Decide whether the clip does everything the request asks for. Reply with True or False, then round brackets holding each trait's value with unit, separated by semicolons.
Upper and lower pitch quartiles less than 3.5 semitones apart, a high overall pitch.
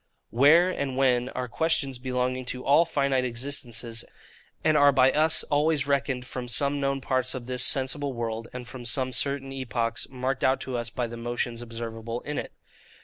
False (2.4 semitones; 130 Hz)